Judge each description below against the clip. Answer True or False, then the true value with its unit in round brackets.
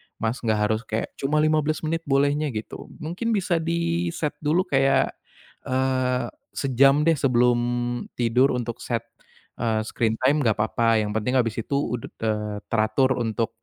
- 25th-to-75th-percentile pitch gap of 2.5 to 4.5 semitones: False (4.9 semitones)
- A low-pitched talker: True (130 Hz)